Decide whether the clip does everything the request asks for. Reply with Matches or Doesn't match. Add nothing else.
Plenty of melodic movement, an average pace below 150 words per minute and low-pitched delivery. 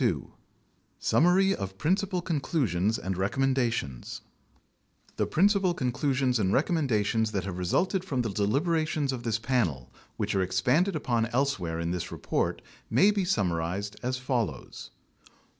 Matches